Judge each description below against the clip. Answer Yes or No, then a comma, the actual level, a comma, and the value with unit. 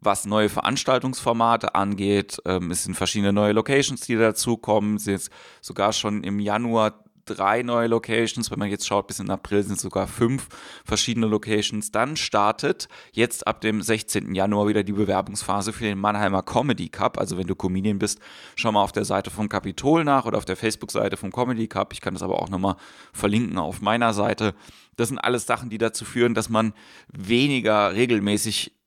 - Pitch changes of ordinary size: No, narrow, 2.2 semitones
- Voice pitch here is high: No, low, 105 Hz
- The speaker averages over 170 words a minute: Yes, fast, 190 wpm